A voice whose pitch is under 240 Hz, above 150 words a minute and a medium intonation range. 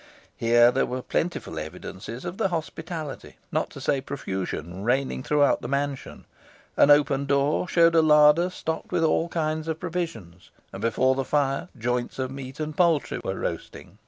Yes: medium, 140 Hz; average, 165 wpm; average, 4.2 semitones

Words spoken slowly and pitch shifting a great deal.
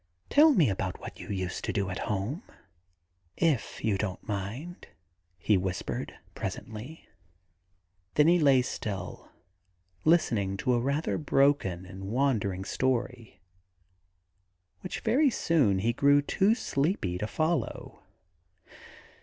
Yes: slow, 120 wpm; wide, 7.9 semitones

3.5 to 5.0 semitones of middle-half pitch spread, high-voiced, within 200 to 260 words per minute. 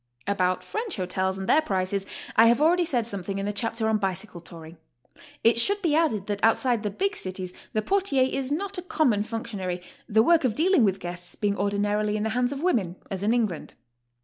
No: wide, 5.5 semitones; high, 215 Hz; fast, 205 wpm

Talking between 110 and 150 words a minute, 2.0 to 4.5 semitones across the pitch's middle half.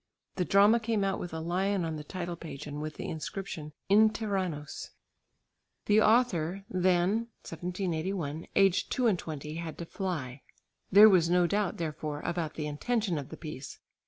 No: average, 165 wpm; average, 4.2 semitones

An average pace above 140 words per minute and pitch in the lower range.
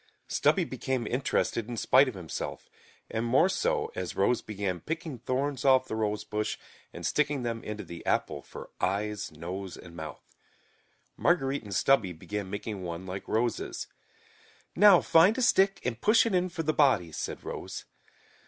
Yes: average, 160 wpm; low, 115 Hz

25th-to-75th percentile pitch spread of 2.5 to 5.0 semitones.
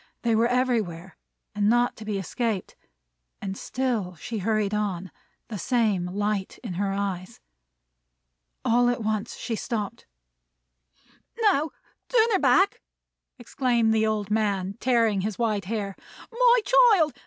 Yes: average, 3.5 semitones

